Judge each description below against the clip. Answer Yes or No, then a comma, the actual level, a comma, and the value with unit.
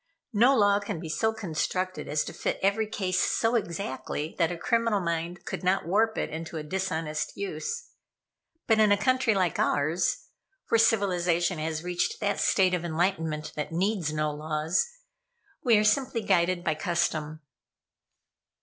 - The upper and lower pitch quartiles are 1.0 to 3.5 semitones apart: No, average, 4.9 semitones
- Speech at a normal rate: Yes, average, 160 wpm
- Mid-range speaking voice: Yes, medium, 180 Hz